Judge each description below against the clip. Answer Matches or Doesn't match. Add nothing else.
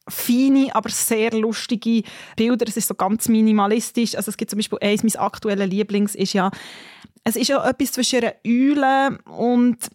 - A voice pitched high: Matches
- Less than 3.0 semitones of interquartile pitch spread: Matches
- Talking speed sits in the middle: Matches